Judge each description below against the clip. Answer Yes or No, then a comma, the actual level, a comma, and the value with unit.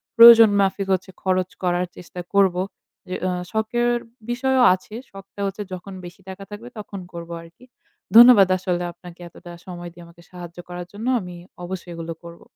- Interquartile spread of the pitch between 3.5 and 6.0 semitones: No, average, 2.9 semitones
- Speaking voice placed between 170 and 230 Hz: Yes, medium, 185 Hz